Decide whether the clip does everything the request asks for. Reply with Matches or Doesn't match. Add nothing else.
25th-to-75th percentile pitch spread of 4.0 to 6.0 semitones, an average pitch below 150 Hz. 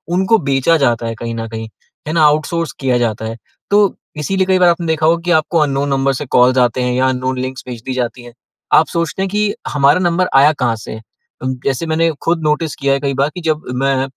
Matches